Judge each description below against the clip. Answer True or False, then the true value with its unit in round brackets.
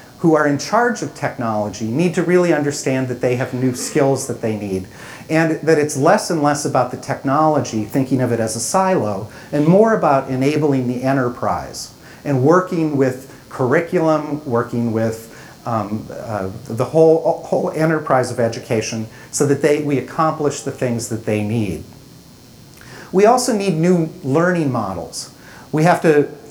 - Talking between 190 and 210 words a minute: False (165 wpm)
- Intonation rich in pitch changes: False (4.7 semitones)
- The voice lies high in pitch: False (140 Hz)